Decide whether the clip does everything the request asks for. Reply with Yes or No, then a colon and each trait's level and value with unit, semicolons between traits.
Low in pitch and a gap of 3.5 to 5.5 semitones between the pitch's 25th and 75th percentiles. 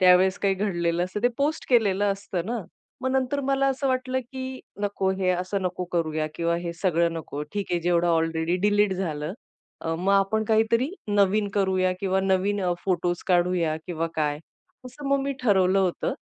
No: high, 190 Hz; average, 3.9 semitones